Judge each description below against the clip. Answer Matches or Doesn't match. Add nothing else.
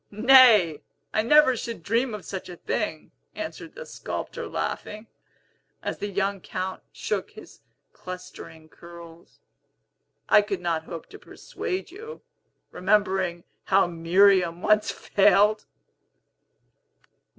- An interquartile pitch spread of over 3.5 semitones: Matches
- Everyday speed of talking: Doesn't match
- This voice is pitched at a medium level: Doesn't match